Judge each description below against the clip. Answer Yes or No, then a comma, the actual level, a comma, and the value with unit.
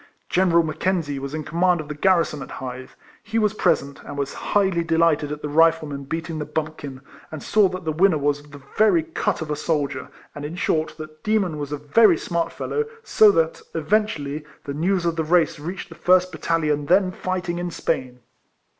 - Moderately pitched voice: Yes, medium, 160 Hz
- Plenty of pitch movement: No, average, 3.5 semitones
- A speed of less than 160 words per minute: No, average, 200 wpm